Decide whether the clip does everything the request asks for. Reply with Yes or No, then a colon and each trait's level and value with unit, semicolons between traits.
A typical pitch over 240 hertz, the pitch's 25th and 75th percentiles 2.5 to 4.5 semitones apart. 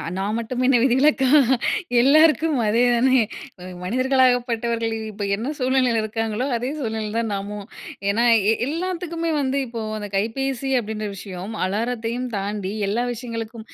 No: high, 235 Hz; average, 3.3 semitones